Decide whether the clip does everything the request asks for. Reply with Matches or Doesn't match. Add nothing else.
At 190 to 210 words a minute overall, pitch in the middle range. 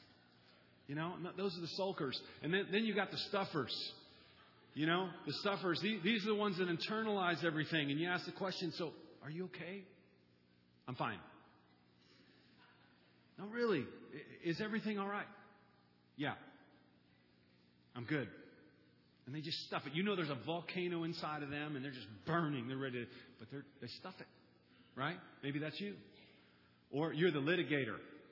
Doesn't match